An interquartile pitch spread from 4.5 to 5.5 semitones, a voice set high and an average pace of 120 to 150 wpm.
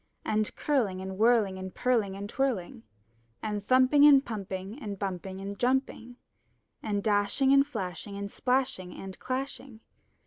Yes: average, 4.8 semitones; high, 210 Hz; average, 140 wpm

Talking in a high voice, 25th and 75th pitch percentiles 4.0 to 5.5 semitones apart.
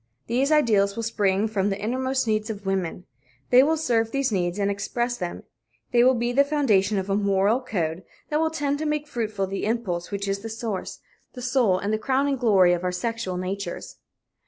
Yes: high, 215 Hz; average, 4.5 semitones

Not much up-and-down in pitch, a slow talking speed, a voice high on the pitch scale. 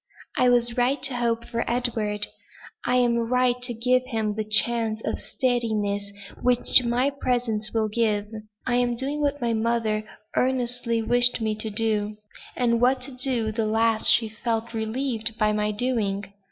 No: narrow, 2.2 semitones; average, 160 wpm; high, 235 Hz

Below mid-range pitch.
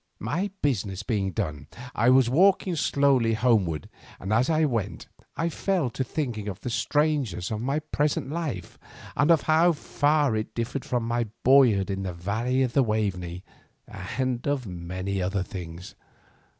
Yes: low, 120 Hz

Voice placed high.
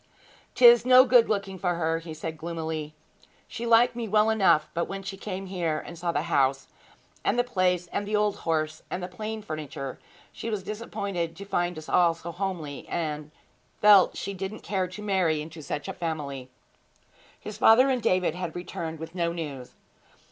No: medium, 180 Hz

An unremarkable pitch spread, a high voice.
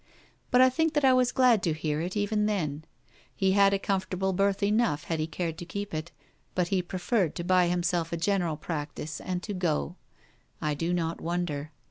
No: average, 3.6 semitones; medium, 180 Hz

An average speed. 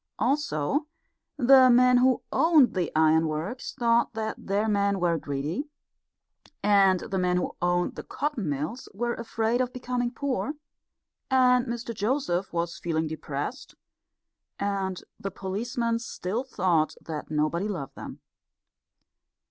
No: slow, 125 wpm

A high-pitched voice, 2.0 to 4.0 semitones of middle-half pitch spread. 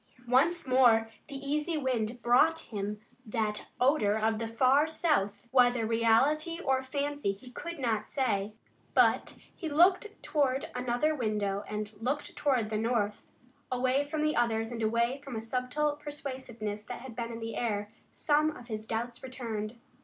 No: high, 245 Hz; average, 4.4 semitones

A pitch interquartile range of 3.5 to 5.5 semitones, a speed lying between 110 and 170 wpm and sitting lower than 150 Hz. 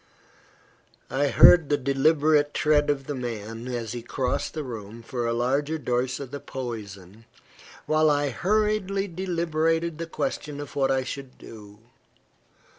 Yes: average, 4.4 semitones; average, 145 wpm; medium, 140 Hz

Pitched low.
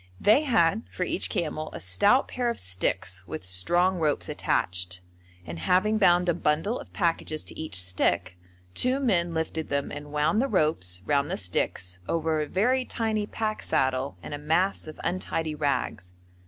No: medium, 160 Hz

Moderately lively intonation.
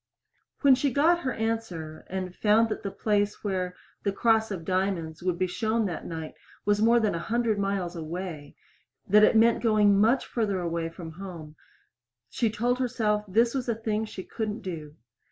Yes: average, 3.9 semitones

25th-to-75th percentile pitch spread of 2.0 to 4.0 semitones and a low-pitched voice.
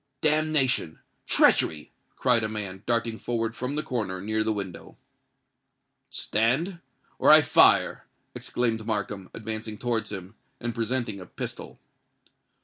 Yes: average, 2.8 semitones; low, 115 Hz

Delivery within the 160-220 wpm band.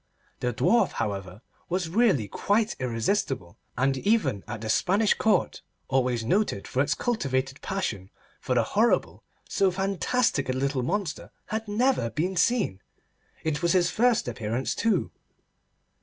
No: average, 140 wpm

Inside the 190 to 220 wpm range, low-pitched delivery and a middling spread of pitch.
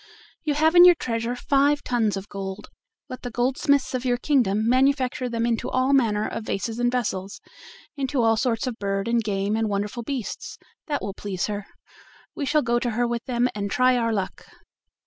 No: average, 195 wpm; high, 240 Hz; average, 3.5 semitones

